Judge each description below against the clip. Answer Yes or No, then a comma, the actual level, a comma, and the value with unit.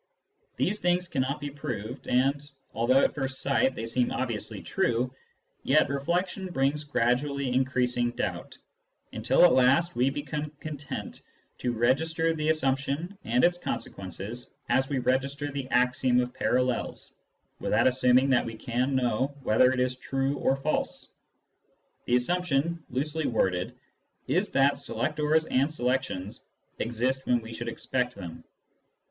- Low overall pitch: Yes, low, 130 Hz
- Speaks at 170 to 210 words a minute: No, average, 140 wpm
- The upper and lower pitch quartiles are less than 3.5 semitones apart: Yes, average, 2.9 semitones